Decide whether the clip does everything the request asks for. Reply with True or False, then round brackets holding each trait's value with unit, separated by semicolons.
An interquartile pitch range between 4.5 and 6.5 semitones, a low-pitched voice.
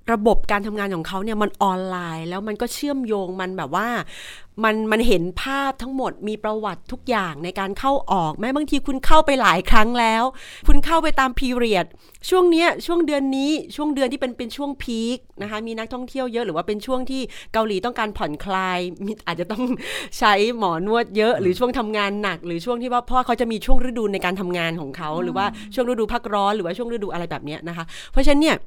False (4.8 semitones; 225 Hz)